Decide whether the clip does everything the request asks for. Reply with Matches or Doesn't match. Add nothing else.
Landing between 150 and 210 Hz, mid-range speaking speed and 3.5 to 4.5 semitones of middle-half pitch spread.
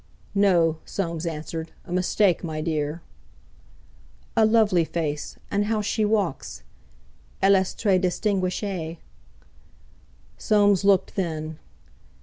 Doesn't match